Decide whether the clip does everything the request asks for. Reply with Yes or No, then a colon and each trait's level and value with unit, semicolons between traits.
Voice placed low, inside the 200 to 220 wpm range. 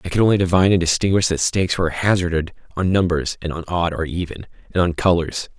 Yes: very low, 90 Hz; fast, 205 wpm